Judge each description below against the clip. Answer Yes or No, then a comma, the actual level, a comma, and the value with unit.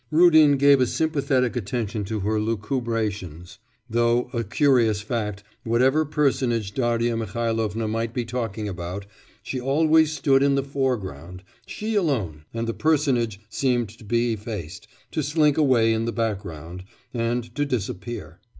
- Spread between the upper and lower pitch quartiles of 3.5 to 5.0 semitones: Yes, average, 4.1 semitones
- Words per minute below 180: Yes, average, 140 wpm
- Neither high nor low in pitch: No, low, 115 Hz